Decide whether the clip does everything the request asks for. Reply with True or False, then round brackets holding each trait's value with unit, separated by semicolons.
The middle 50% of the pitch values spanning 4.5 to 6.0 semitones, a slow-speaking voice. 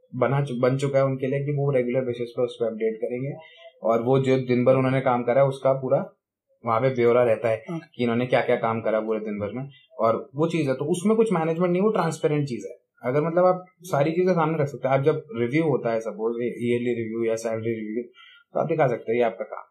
False (4.9 semitones; 245 wpm)